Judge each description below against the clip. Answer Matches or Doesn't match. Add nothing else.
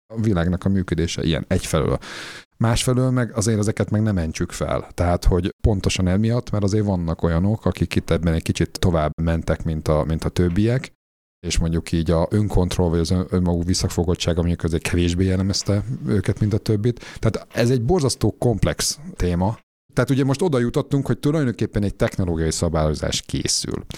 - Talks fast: Matches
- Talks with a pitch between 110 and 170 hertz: Doesn't match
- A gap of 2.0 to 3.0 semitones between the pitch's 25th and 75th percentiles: Doesn't match